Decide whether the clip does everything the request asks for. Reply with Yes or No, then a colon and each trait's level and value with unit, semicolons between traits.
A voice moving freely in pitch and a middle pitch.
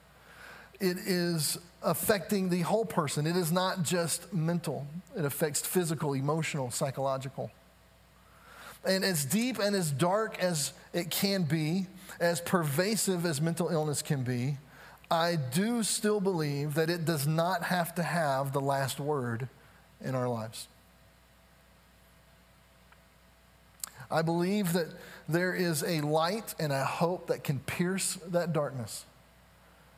No: average, 4.6 semitones; medium, 165 Hz